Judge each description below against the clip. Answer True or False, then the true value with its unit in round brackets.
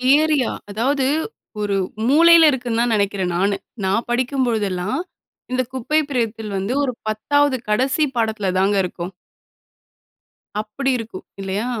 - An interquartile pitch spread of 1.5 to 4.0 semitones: False (4.7 semitones)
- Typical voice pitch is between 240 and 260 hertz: False (230 Hz)